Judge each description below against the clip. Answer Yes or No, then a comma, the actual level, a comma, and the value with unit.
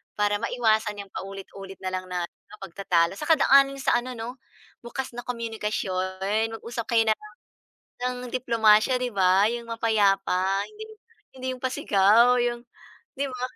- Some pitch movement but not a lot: Yes, average, 4.0 semitones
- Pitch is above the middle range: Yes, high, 225 Hz